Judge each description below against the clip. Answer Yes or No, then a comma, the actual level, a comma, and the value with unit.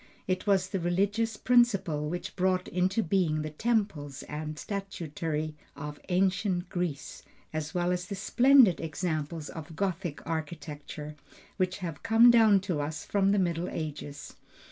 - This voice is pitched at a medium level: Yes, medium, 180 Hz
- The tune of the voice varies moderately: Yes, average, 4.2 semitones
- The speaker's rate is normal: Yes, average, 145 wpm